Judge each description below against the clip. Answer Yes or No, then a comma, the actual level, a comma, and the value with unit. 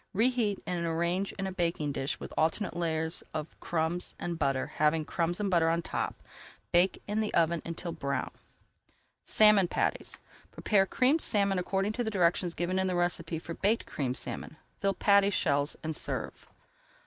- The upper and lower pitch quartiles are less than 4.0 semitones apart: Yes, average, 3.4 semitones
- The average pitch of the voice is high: No, medium, 175 Hz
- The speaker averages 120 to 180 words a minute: Yes, average, 165 wpm